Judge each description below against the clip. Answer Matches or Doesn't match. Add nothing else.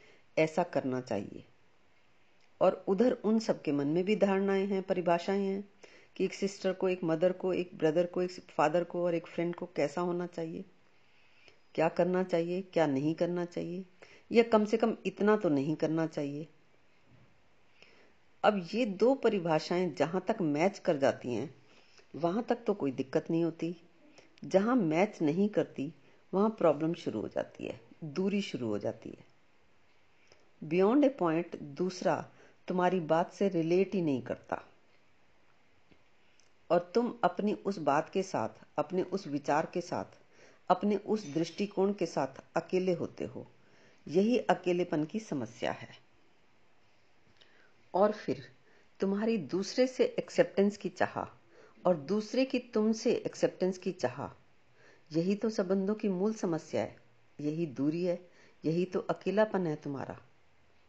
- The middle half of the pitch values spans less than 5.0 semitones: Matches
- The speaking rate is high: Doesn't match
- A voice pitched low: Doesn't match